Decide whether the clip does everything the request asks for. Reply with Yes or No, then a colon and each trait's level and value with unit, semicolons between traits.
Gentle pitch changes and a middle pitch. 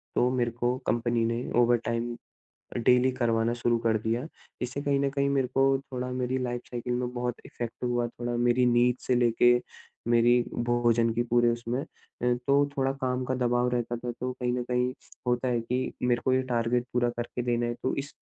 No: narrow, 1.0 semitones; low, 120 Hz